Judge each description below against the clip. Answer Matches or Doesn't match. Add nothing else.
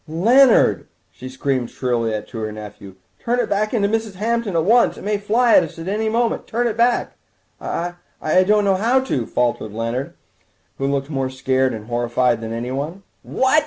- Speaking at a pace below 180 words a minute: Doesn't match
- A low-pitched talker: Doesn't match